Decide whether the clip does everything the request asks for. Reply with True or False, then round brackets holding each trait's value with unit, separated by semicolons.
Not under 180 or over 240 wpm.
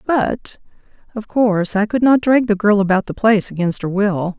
True (205 wpm)